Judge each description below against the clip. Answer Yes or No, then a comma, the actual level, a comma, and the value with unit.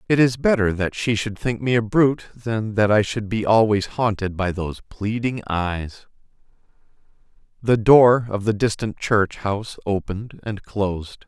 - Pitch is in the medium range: No, low, 110 Hz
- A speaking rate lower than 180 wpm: Yes, average, 165 wpm